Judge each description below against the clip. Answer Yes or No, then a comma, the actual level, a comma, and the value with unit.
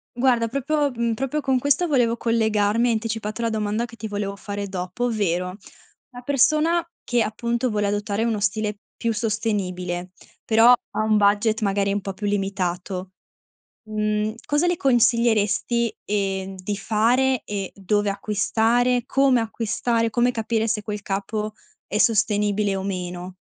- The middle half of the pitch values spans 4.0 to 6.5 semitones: No, average, 2.7 semitones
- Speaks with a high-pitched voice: Yes, high, 215 Hz